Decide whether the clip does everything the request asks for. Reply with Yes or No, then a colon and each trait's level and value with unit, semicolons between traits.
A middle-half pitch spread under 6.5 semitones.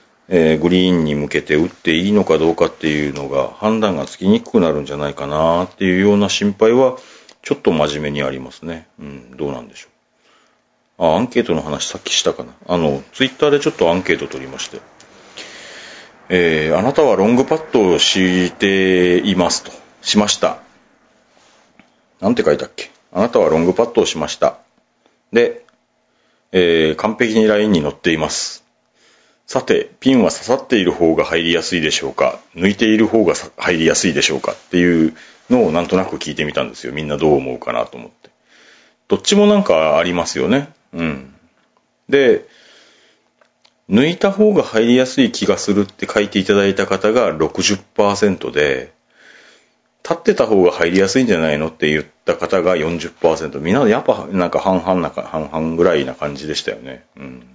Yes: wide, 5.6 semitones